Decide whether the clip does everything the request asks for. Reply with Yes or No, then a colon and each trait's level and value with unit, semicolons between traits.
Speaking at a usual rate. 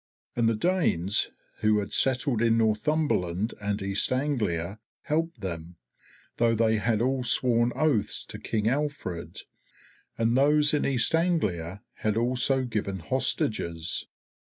No: slow, 130 wpm